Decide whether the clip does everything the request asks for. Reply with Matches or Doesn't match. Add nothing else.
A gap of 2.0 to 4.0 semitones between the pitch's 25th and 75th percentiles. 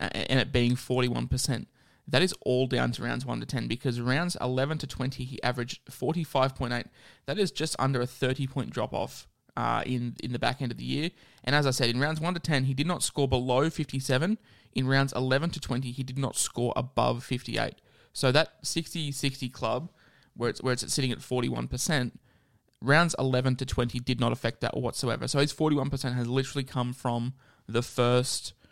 Matches